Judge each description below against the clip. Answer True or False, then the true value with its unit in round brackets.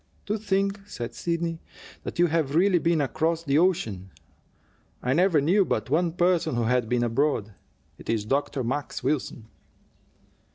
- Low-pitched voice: False (155 Hz)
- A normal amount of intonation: False (5.7 semitones)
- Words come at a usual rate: True (155 wpm)